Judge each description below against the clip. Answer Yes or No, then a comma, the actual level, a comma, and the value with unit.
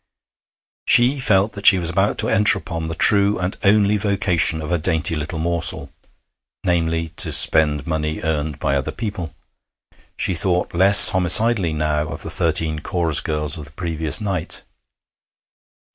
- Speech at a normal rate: Yes, average, 155 wpm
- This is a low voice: Yes, very low, 85 Hz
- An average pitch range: Yes, average, 3.7 semitones